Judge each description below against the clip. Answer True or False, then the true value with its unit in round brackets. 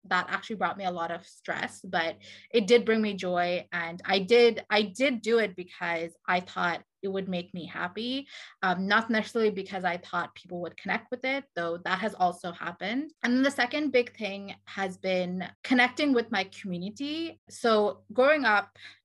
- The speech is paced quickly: False (190 wpm)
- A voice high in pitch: True (195 Hz)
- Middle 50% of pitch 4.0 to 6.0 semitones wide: True (4.7 semitones)